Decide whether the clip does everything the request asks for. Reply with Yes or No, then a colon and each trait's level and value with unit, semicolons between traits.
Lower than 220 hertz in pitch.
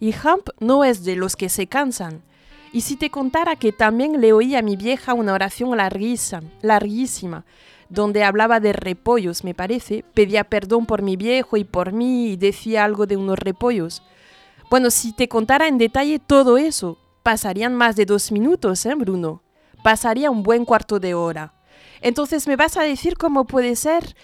No: high, 225 Hz